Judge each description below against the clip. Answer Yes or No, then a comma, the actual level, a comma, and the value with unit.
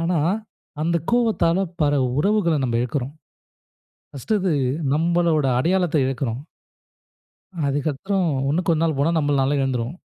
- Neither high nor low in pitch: Yes, medium, 155 Hz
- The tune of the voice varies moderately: Yes, average, 4.0 semitones